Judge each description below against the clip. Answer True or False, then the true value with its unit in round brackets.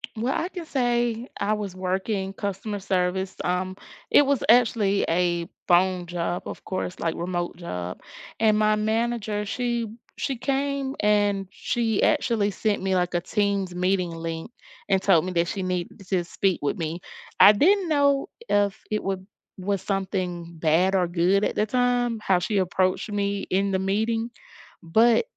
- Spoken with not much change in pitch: False (3.7 semitones)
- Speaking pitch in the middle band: False (195 Hz)